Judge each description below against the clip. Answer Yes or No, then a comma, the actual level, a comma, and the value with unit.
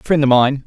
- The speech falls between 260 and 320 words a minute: Yes, fast, 270 wpm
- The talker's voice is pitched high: No, medium, 140 Hz